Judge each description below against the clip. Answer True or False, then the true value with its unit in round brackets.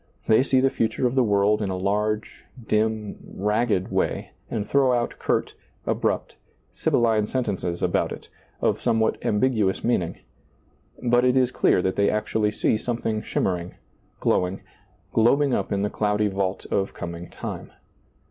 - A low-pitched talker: True (105 Hz)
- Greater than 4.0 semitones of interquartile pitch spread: False (3.3 semitones)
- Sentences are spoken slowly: False (155 wpm)